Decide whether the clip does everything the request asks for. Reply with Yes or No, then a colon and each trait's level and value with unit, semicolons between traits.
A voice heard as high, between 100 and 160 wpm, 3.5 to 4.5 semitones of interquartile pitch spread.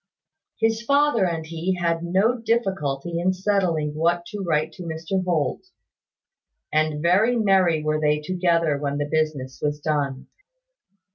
No: medium, 170 Hz; average, 140 wpm; average, 3.8 semitones